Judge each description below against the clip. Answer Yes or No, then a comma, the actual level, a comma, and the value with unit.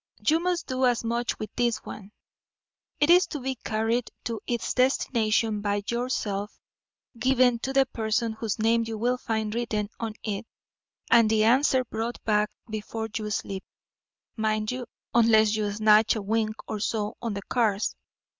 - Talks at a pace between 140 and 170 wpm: Yes, average, 165 wpm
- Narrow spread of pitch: Yes, narrow, 2.1 semitones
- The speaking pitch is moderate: No, high, 225 Hz